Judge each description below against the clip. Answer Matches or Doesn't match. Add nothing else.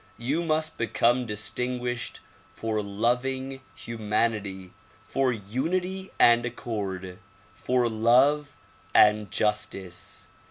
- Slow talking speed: Matches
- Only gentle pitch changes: Doesn't match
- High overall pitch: Doesn't match